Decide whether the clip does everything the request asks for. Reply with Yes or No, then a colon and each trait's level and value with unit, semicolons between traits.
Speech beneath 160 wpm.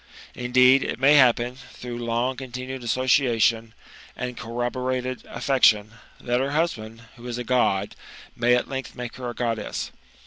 Yes: average, 145 wpm